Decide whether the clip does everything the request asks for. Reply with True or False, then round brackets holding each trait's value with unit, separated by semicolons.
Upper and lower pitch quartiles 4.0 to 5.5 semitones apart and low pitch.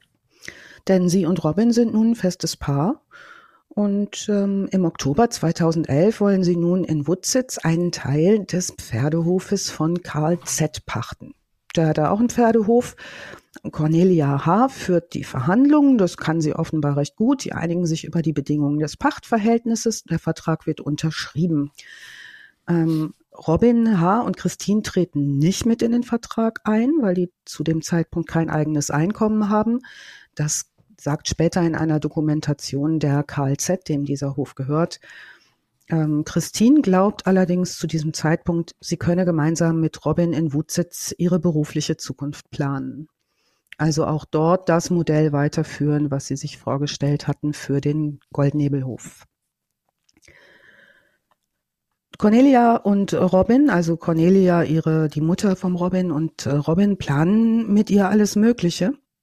False (4.8 semitones; 170 Hz)